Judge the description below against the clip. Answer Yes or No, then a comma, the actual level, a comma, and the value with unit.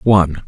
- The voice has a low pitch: Yes, very low, 95 Hz